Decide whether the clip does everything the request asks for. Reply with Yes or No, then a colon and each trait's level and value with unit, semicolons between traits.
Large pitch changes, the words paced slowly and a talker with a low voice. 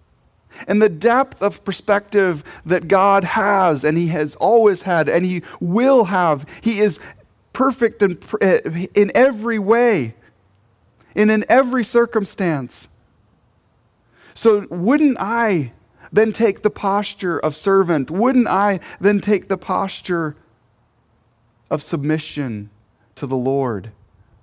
No: wide, 6.6 semitones; slow, 120 wpm; medium, 185 Hz